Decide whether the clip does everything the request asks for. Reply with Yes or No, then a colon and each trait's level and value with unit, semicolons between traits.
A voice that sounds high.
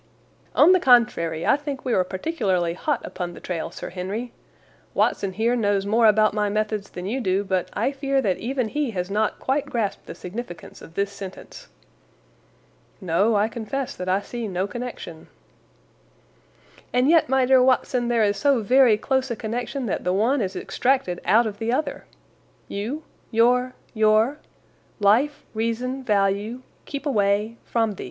Yes: high, 225 Hz